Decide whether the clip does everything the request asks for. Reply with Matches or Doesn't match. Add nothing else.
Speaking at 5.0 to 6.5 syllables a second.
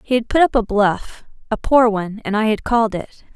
Matches